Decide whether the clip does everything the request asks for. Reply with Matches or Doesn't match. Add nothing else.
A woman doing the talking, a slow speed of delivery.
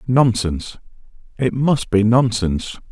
Doesn't match